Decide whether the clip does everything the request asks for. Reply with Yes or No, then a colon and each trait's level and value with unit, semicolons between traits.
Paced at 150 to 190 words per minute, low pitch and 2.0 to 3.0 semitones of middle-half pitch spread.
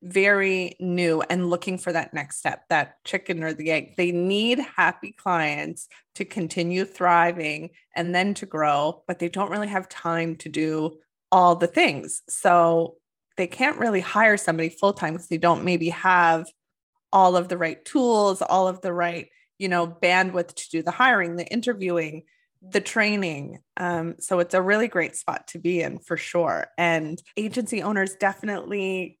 No: average, 170 wpm; medium, 180 Hz; narrow, 2.6 semitones